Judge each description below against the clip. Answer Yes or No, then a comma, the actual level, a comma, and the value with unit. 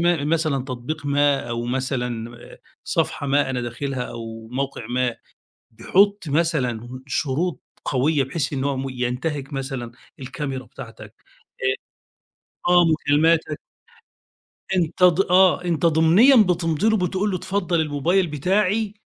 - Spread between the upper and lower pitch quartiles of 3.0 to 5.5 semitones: Yes, average, 5.0 semitones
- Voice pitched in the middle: Yes, medium, 145 Hz